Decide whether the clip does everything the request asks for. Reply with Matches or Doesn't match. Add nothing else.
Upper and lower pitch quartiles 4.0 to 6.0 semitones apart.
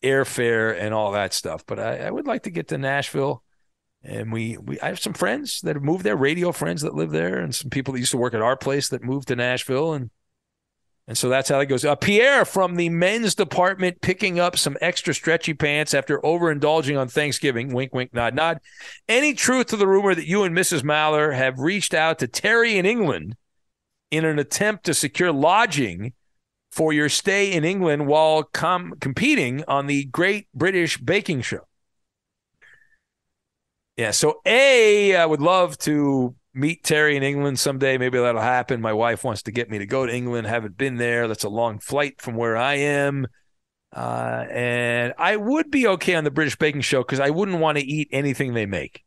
Matches